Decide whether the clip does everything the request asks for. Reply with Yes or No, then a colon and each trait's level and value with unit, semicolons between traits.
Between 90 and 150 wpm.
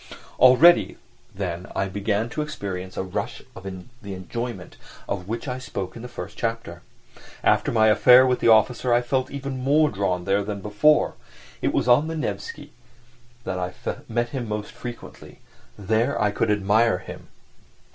No: average, 165 wpm